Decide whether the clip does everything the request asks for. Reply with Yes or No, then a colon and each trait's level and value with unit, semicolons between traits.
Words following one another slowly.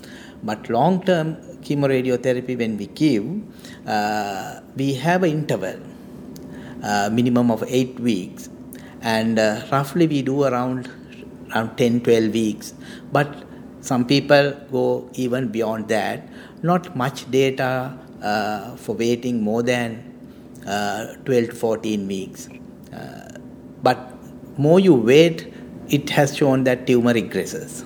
Yes: slow, 125 wpm